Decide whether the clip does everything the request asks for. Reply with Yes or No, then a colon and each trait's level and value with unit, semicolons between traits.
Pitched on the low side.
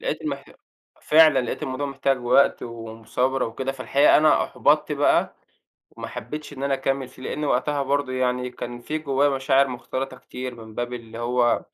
Yes: low, 130 Hz